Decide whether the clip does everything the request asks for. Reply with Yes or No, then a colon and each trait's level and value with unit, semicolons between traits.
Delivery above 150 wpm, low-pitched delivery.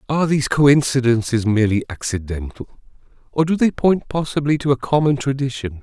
No: average, 145 wpm; low, 130 Hz